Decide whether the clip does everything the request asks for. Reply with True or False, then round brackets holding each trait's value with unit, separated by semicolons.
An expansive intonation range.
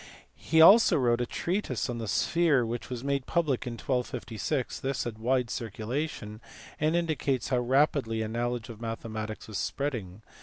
False (3.8 semitones)